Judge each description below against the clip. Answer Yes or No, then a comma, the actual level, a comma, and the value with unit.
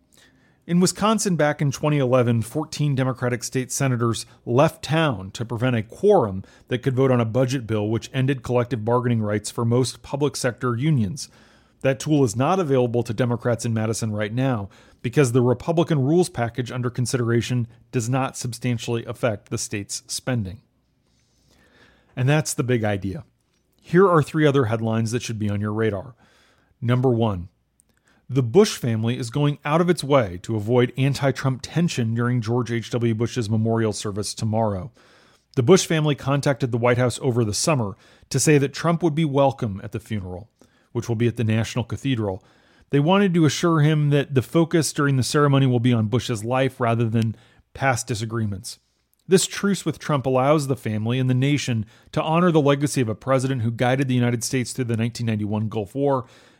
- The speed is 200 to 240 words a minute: No, average, 180 wpm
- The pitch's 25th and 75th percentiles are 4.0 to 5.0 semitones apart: No, average, 3.4 semitones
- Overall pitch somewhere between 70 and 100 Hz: No, low, 125 Hz